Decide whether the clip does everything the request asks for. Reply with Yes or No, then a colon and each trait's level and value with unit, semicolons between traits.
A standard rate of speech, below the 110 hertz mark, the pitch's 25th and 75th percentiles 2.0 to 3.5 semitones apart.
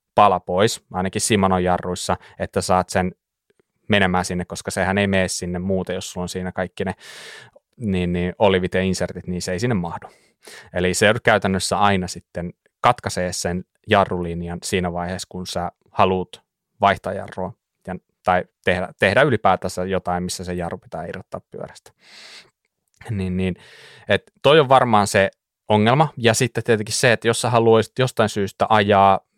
No: fast, 160 wpm; very low, 95 Hz; average, 2.8 semitones